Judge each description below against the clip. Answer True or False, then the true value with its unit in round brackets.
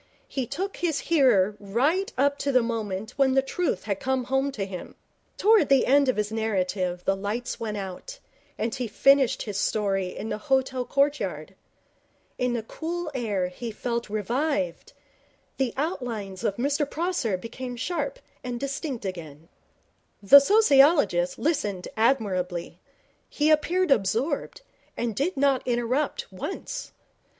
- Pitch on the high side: True (245 Hz)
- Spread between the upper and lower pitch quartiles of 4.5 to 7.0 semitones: True (5.6 semitones)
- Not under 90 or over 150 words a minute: True (140 wpm)